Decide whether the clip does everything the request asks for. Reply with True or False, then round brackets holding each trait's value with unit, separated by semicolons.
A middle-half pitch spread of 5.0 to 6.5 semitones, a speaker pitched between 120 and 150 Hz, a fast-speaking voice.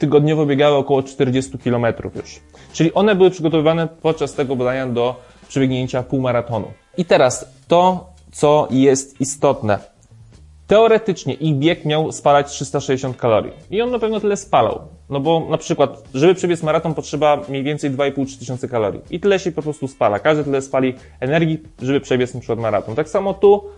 False (4.0 semitones; 140 Hz; 165 wpm)